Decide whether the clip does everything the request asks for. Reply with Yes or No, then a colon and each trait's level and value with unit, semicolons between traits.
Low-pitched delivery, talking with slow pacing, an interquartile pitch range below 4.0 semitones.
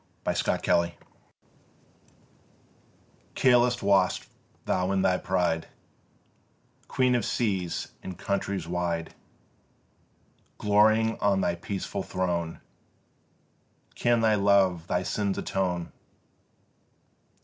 Yes: very low, 95 Hz; slow, 85 wpm; average, 2.8 semitones